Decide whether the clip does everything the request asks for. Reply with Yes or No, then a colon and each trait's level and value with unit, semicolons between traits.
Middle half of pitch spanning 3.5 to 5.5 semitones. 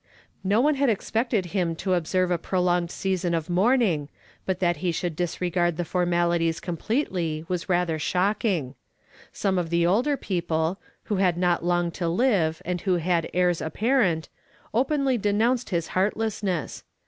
No: average, 3.1 semitones